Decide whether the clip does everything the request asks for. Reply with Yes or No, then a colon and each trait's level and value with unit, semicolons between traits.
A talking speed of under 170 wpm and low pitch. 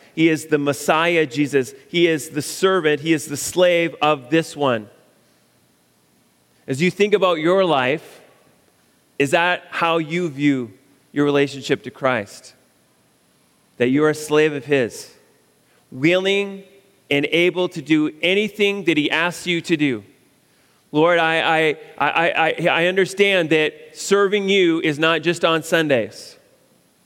No: average, 145 wpm; medium, 160 Hz